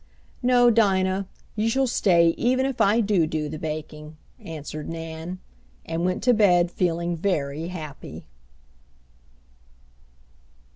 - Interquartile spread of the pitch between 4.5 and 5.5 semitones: Yes, average, 4.9 semitones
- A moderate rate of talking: No, slow, 115 wpm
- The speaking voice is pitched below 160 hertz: No, medium, 175 Hz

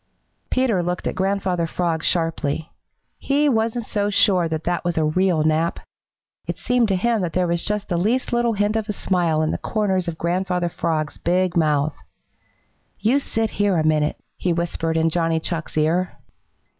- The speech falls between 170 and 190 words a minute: Yes, average, 180 wpm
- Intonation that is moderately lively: Yes, average, 4.0 semitones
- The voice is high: No, medium, 180 Hz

